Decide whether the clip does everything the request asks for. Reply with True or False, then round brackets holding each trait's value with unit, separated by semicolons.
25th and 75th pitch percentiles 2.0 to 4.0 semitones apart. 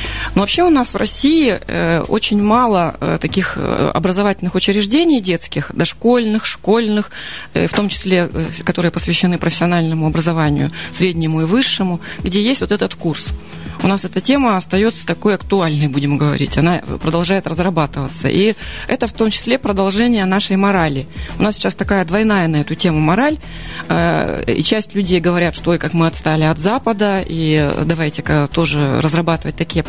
False (4.4 semitones)